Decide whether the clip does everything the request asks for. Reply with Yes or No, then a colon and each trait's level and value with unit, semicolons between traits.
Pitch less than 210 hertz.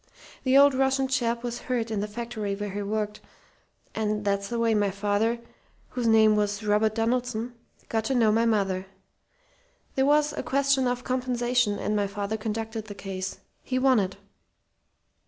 No: high, 225 Hz